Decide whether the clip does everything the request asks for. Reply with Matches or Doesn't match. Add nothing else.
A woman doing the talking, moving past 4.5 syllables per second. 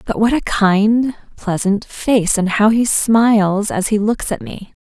Doesn't match